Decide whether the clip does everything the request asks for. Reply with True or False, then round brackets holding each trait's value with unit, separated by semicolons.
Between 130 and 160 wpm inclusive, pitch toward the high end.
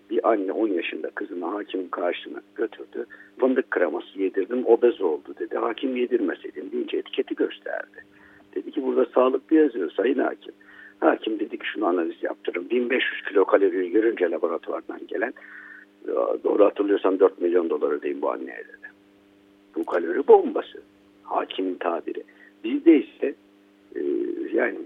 True (135 wpm; 365 Hz)